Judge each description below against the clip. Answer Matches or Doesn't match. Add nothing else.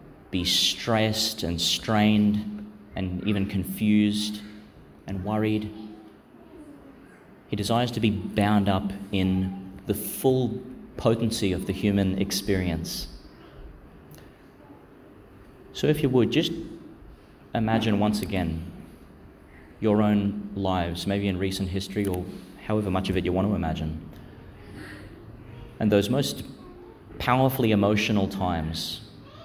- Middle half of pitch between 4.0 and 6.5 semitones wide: Doesn't match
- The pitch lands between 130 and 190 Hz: Doesn't match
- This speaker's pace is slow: Matches